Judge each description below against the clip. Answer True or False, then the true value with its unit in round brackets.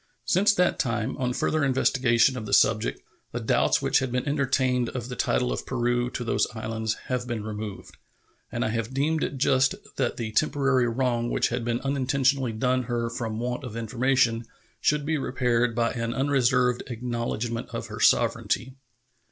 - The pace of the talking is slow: False (175 wpm)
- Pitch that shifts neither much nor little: False (2.2 semitones)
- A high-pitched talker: False (125 Hz)